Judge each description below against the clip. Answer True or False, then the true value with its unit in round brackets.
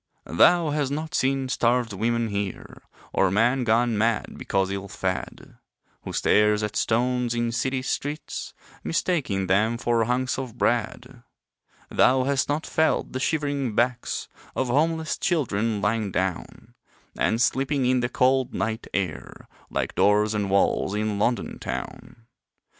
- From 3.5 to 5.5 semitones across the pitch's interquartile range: True (3.9 semitones)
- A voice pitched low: True (120 Hz)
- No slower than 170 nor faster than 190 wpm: False (140 wpm)